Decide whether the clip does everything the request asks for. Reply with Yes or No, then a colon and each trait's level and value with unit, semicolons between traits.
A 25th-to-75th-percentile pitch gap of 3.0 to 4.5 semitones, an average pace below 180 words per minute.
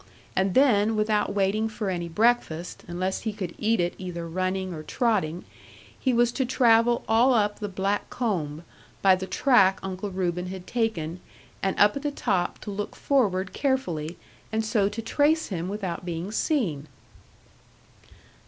Yes: average, 4.0 semitones; average, 160 wpm